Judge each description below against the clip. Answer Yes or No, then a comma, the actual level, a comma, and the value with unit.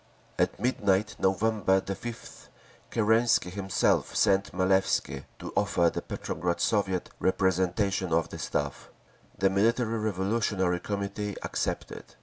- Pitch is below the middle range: Yes, low, 100 Hz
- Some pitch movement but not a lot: No, narrow, 2.3 semitones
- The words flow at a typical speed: No, slow, 110 wpm